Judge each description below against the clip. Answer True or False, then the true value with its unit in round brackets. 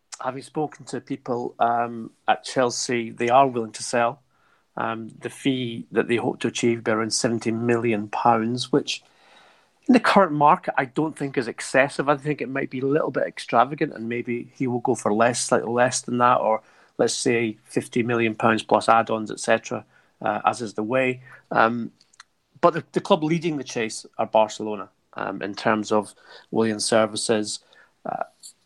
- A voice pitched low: True (120 Hz)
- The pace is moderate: True (180 wpm)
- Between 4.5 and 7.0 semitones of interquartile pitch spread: False (3.3 semitones)